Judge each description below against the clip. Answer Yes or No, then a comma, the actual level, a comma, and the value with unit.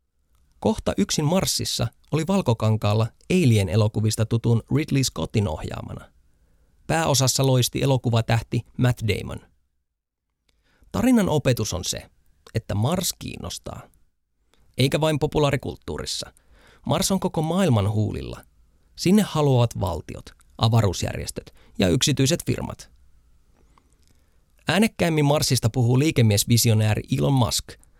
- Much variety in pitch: Yes, wide, 8.1 semitones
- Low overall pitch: Yes, low, 115 Hz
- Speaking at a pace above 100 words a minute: No, slow, 95 wpm